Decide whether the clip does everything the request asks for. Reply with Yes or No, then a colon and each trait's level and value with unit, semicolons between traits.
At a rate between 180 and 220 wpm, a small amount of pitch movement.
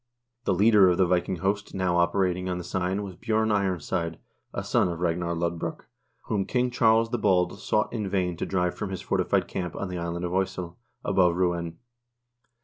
Yes: average, 195 wpm; narrow, 2.3 semitones